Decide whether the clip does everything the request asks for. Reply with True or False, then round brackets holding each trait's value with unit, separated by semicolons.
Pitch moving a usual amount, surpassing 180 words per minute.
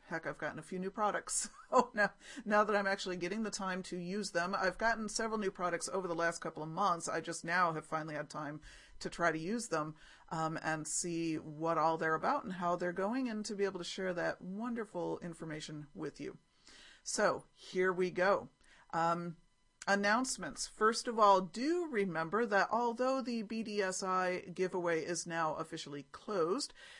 True (3.9 semitones; 190 wpm)